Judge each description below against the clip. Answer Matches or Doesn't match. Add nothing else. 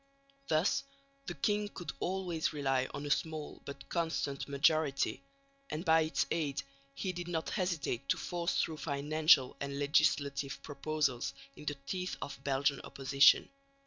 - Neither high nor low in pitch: Matches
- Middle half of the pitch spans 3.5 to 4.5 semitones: Doesn't match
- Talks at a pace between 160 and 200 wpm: Doesn't match